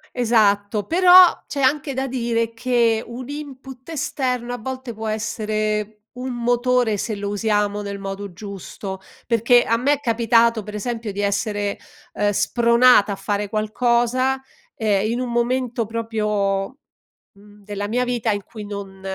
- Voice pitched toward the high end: Yes, high, 225 Hz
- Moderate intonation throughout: Yes, average, 3.1 semitones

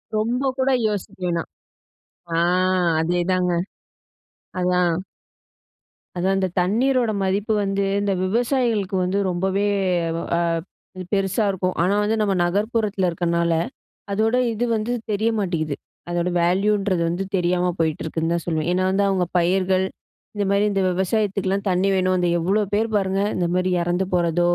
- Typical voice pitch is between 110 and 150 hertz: No, high, 190 Hz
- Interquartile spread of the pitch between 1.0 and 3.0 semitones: Yes, narrow, 2.6 semitones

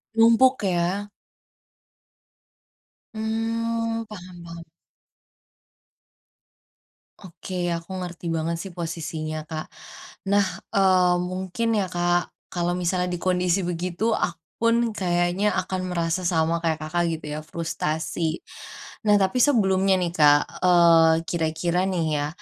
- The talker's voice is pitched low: No, medium, 175 Hz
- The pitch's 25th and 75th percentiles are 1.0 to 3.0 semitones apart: Yes, narrow, 2.6 semitones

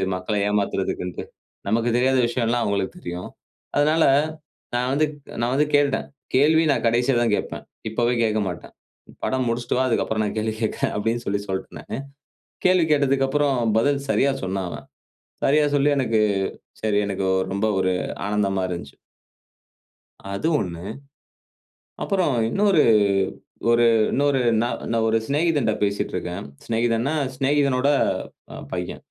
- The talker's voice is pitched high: No, low, 120 Hz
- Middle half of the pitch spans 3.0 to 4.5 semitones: No, average, 5.1 semitones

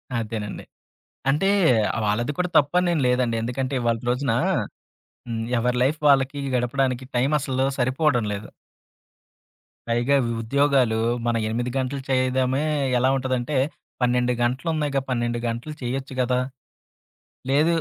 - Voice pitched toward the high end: No, low, 130 Hz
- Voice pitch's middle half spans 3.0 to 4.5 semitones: No, narrow, 2.4 semitones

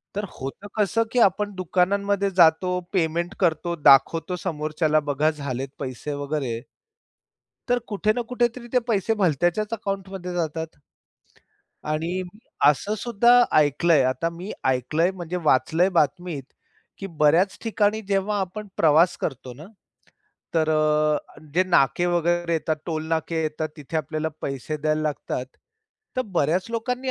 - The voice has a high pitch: No, medium, 170 Hz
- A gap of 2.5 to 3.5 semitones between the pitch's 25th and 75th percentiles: No, average, 4.3 semitones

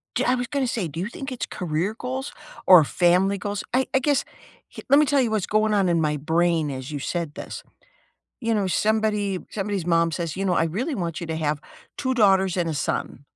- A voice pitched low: No, high, 190 Hz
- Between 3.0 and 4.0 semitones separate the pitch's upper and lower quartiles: No, average, 5.1 semitones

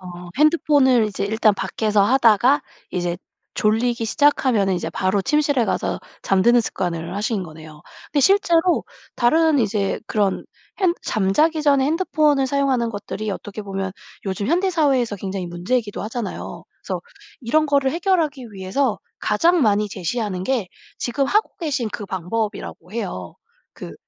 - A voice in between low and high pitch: No, high, 225 Hz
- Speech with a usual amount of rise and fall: No, wide, 6.5 semitones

